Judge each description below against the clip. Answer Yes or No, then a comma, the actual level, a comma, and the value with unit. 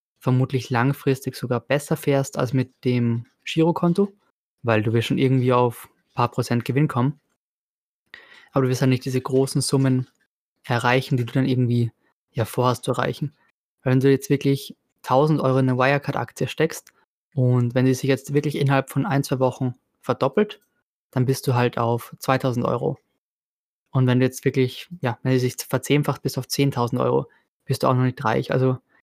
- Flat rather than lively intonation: Yes, narrow, 1.7 semitones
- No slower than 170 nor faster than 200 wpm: Yes, average, 180 wpm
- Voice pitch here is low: Yes, low, 130 Hz